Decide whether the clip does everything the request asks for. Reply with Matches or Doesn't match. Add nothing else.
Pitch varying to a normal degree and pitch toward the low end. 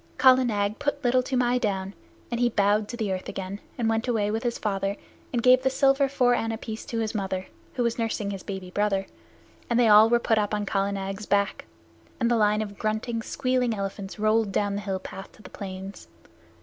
Doesn't match